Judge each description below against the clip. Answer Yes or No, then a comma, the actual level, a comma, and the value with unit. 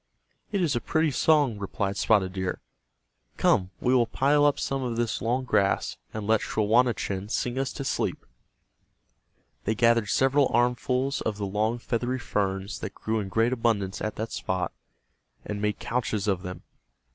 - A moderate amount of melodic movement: Yes, average, 3.8 semitones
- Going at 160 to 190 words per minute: Yes, average, 165 wpm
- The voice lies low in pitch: Yes, low, 115 Hz